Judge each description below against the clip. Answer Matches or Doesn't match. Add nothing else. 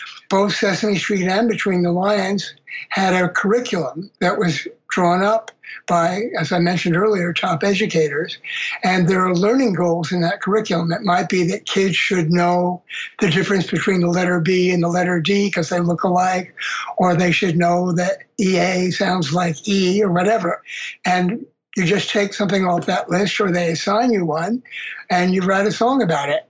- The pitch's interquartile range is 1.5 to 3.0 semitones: Matches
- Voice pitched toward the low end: Doesn't match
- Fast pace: Doesn't match